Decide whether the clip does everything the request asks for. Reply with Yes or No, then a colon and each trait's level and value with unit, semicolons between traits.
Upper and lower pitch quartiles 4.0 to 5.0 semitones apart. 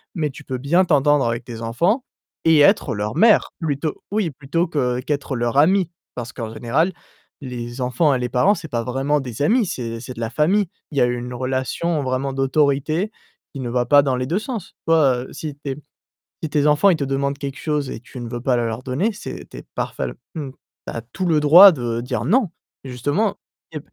Yes: average, 4.5 semitones